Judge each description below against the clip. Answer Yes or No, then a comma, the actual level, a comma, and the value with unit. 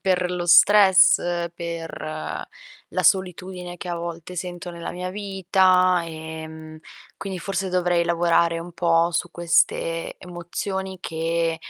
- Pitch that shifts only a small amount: Yes, narrow, 1.6 semitones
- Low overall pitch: No, medium, 175 Hz